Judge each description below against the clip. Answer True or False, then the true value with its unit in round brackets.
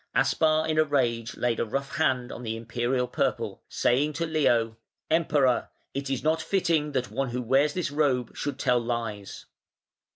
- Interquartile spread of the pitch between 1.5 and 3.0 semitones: False (4.1 semitones)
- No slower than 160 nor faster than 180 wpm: True (170 wpm)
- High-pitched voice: False (135 Hz)